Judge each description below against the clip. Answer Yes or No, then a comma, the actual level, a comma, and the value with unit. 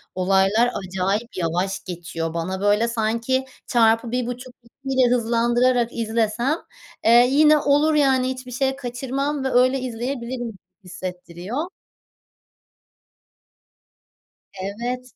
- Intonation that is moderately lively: Yes, average, 4.1 semitones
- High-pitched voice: Yes, high, 235 Hz